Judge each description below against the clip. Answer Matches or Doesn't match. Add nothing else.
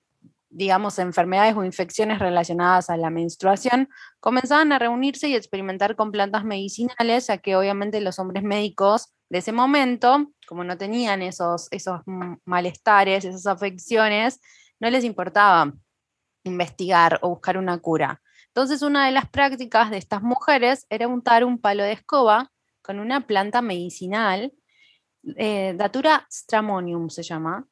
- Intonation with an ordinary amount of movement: Matches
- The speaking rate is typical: Matches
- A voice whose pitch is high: Matches